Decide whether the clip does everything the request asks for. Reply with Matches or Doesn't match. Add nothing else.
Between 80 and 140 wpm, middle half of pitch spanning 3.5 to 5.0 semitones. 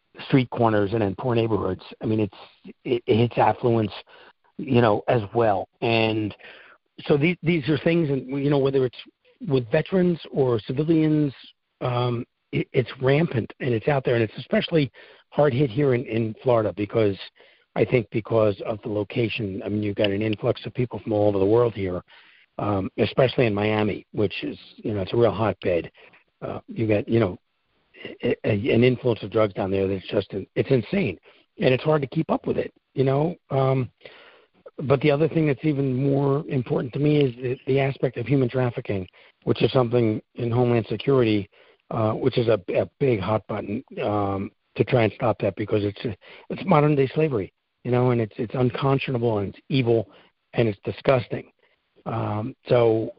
Doesn't match